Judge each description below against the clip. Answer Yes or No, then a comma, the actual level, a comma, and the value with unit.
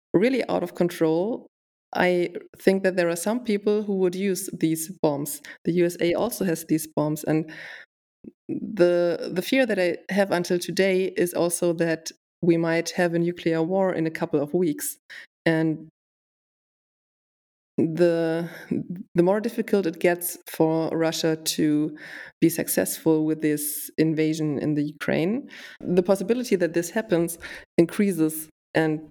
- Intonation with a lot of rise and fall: No, average, 2.7 semitones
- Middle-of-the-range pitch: Yes, medium, 170 Hz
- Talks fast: No, average, 145 wpm